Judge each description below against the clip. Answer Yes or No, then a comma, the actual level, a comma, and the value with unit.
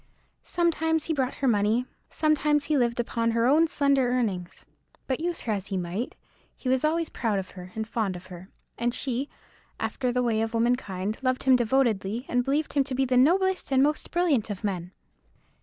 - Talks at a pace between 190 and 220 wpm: Yes, average, 195 wpm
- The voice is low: No, very high, 250 Hz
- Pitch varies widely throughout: No, average, 4.6 semitones